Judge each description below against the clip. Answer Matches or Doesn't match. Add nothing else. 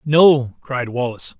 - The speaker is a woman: Doesn't match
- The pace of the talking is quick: Doesn't match